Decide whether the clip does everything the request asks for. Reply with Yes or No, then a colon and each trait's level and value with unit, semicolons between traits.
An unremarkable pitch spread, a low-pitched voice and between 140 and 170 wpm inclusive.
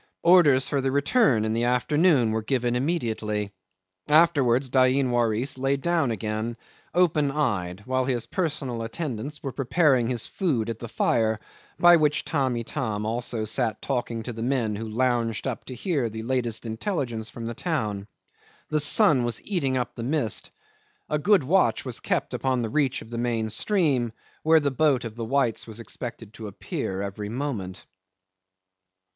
Yes: average, 4.1 semitones; low, 125 Hz; average, 165 wpm